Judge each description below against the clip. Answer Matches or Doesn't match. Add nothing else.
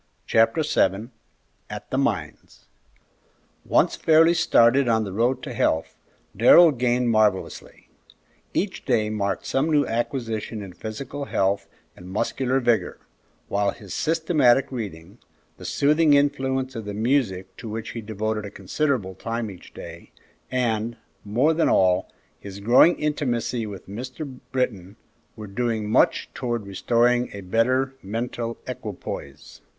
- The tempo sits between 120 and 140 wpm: Matches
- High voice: Doesn't match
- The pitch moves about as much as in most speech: Matches